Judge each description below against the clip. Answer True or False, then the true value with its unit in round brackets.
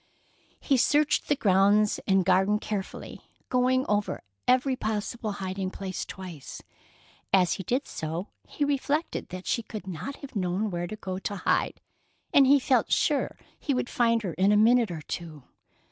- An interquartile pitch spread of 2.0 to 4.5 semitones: False (5.1 semitones)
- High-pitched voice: True (210 Hz)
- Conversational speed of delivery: True (165 wpm)